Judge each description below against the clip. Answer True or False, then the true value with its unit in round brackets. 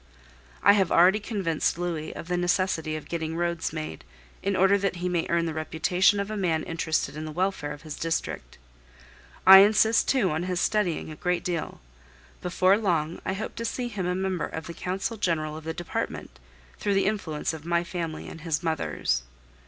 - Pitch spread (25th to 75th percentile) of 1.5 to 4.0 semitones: True (3.2 semitones)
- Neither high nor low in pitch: True (175 Hz)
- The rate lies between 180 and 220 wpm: True (195 wpm)